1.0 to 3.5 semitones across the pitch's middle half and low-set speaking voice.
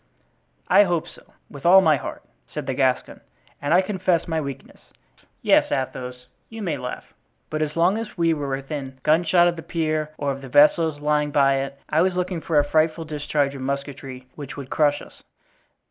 No: average, 3.2 semitones; medium, 150 Hz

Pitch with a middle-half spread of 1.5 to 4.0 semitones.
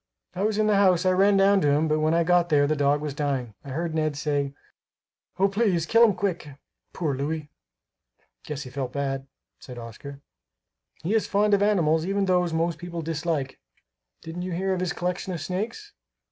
No: average, 4.7 semitones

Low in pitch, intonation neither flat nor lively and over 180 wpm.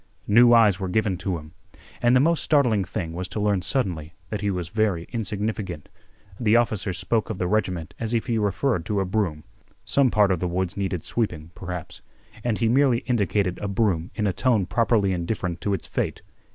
Yes: low, 100 Hz; average, 3.9 semitones; average, 200 wpm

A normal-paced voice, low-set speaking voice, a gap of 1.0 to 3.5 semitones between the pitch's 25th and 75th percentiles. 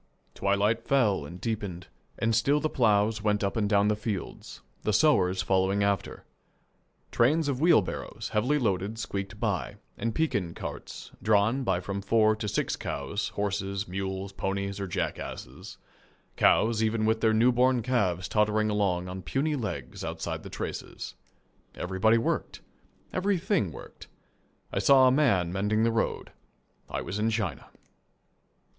Yes: average, 145 wpm; low, 105 Hz; average, 2.9 semitones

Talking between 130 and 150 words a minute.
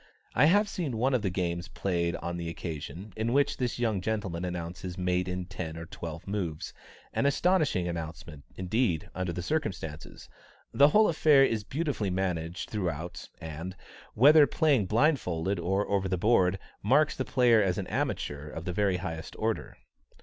No: average, 165 wpm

